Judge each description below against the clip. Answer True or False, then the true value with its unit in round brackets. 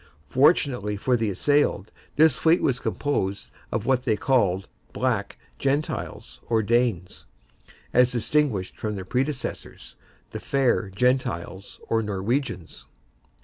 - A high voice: False (120 Hz)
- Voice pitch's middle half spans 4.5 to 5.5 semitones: True (4.9 semitones)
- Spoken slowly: True (115 wpm)